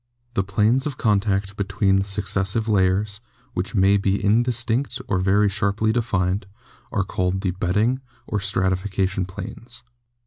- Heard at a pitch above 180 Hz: No, low, 100 Hz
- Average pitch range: No, narrow, 2.3 semitones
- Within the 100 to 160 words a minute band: Yes, slow, 135 wpm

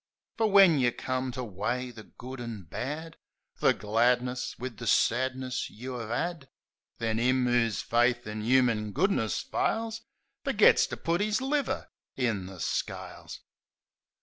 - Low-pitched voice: Yes, low, 125 Hz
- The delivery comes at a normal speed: Yes, average, 150 wpm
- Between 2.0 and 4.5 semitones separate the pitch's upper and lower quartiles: Yes, average, 3.0 semitones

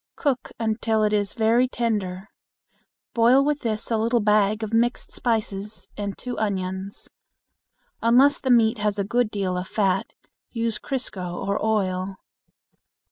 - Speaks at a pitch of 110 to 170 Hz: No, high, 215 Hz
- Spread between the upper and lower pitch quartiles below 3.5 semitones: Yes, average, 2.8 semitones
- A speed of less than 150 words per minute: Yes, average, 140 wpm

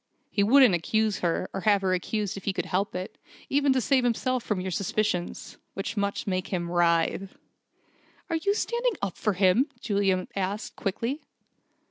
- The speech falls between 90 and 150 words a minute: No, average, 170 wpm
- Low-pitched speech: No, high, 200 Hz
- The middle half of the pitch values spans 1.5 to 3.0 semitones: No, average, 4.2 semitones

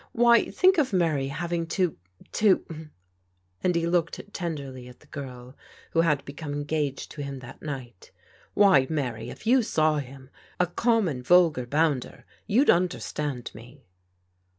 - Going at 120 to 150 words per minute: No, average, 160 wpm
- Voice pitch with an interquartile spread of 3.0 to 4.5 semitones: No, average, 5.1 semitones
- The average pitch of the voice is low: No, medium, 150 Hz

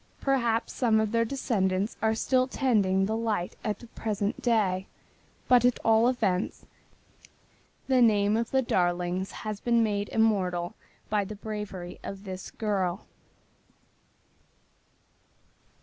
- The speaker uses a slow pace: Yes, slow, 125 wpm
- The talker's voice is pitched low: No, high, 215 Hz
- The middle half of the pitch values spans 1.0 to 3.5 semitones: Yes, average, 3.2 semitones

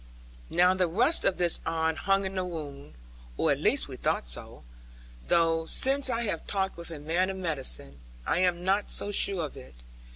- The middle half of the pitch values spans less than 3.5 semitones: Yes, average, 3.1 semitones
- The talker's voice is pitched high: No, medium, 175 Hz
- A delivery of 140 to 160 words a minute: No, average, 195 wpm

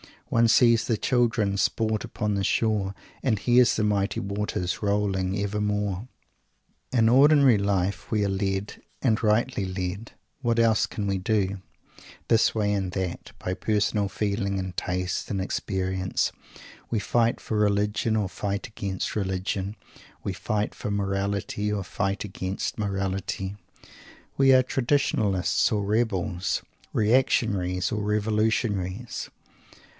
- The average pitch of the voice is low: Yes, low, 105 Hz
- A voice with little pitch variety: Yes, narrow, 2.3 semitones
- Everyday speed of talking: No, slow, 130 wpm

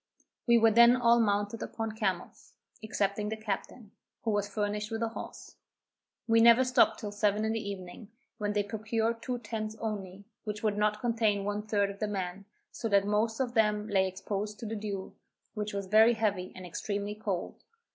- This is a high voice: Yes, high, 210 Hz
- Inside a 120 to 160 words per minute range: No, average, 185 wpm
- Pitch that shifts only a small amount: Yes, narrow, 1.8 semitones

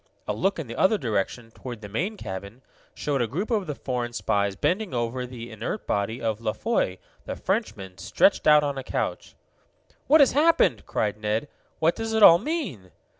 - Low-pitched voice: Yes, low, 125 Hz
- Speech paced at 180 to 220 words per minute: Yes, average, 190 wpm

